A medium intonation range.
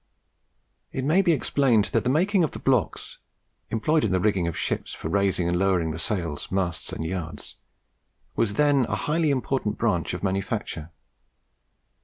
No: wide, 7.4 semitones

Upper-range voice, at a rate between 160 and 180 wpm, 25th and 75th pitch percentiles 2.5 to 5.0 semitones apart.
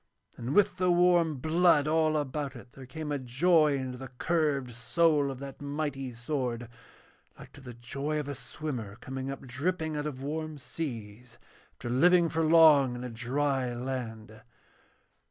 No: medium, 140 Hz; average, 165 wpm; average, 3.9 semitones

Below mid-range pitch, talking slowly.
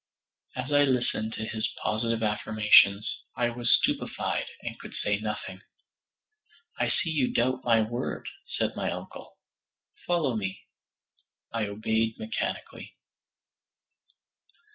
Yes: low, 115 Hz; slow, 115 wpm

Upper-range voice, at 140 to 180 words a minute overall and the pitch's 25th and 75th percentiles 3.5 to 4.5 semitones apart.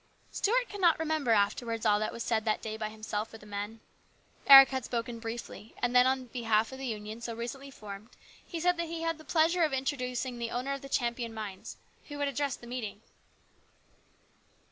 No: high, 245 Hz; fast, 205 wpm; average, 4.0 semitones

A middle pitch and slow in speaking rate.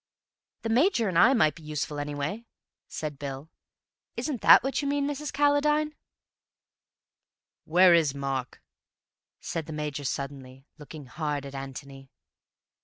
Yes: medium, 155 Hz; slow, 130 wpm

